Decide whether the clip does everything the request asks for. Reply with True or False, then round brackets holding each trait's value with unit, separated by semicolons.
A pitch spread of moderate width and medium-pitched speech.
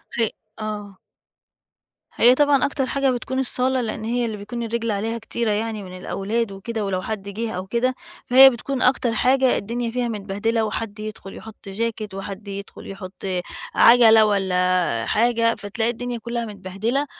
False (3.1 semitones; 225 Hz)